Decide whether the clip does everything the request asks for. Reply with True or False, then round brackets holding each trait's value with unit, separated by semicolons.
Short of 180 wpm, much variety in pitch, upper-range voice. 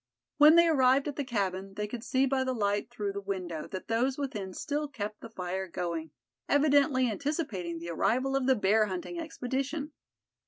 False (185 wpm; 6.1 semitones; 240 Hz)